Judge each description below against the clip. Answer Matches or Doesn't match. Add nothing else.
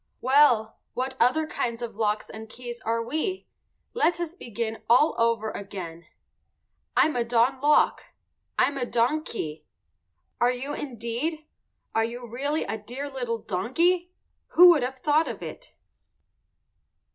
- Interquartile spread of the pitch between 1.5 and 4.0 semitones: Doesn't match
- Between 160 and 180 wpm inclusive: Doesn't match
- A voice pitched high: Matches